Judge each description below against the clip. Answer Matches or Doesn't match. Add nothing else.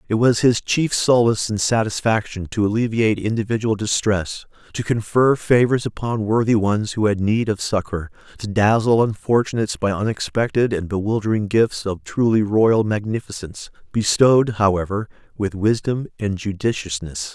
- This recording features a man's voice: Matches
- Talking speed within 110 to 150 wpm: Matches